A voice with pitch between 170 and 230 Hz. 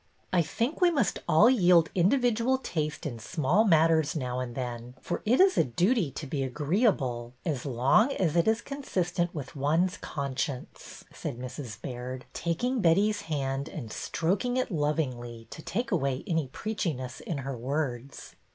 No: medium, 155 Hz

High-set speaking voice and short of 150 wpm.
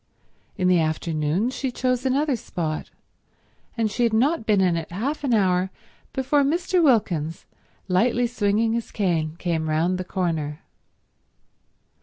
Yes: high, 200 Hz; average, 140 wpm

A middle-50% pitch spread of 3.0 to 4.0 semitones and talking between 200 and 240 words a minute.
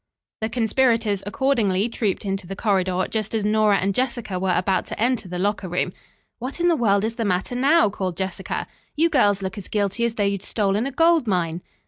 Yes: average, 3.6 semitones; fast, 205 wpm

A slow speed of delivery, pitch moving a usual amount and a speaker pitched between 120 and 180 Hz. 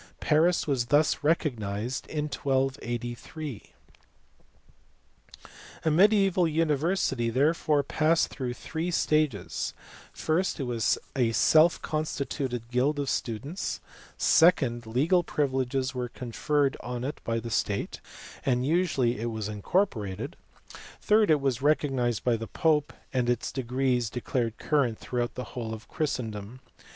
Yes: slow, 120 wpm; average, 4.4 semitones; low, 135 Hz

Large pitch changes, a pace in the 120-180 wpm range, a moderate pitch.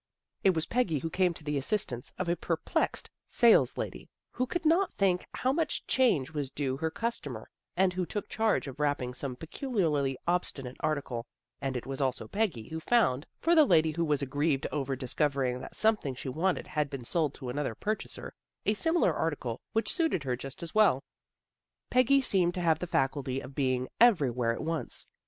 No: wide, 6.9 semitones; average, 195 wpm; medium, 155 Hz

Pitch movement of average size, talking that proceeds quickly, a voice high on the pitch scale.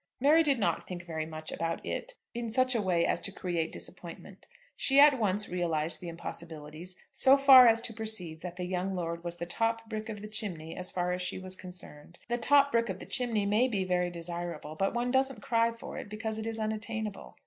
Yes: average, 4.9 semitones; fast, 220 wpm; high, 195 Hz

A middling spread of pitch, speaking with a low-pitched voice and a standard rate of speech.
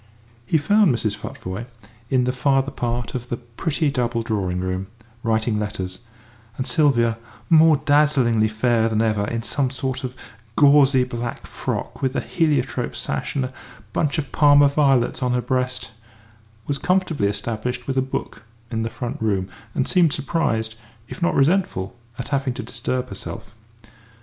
Yes: average, 3.9 semitones; low, 125 Hz; average, 160 wpm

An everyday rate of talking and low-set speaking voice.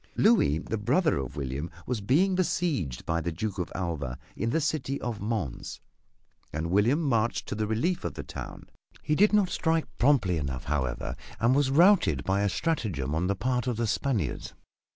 Yes: average, 185 wpm; low, 110 Hz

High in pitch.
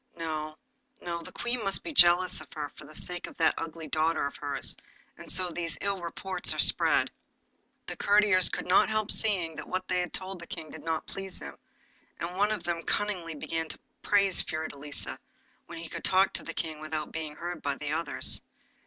No: medium, 170 Hz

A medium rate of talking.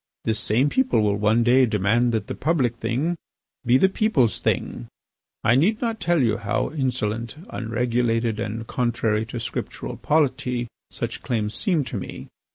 Yes: average, 160 wpm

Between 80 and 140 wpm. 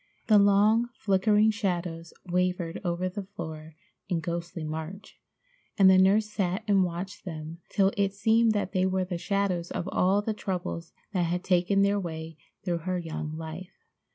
No: average, 165 wpm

